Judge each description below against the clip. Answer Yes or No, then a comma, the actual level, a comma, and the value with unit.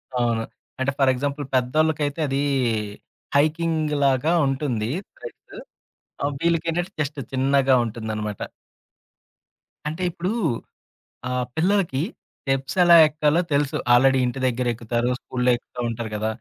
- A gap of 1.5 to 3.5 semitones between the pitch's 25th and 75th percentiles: No, average, 3.9 semitones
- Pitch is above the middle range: No, low, 135 Hz